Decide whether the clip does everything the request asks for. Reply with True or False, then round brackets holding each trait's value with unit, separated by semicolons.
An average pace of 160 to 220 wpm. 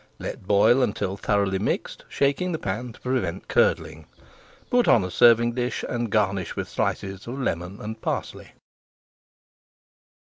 False (140 wpm)